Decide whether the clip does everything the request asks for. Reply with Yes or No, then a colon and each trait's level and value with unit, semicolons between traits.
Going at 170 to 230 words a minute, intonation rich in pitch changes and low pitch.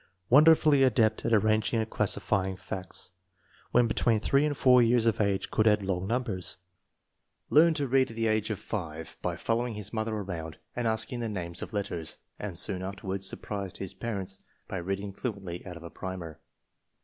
No: average, 180 wpm; average, 3.7 semitones; low, 105 Hz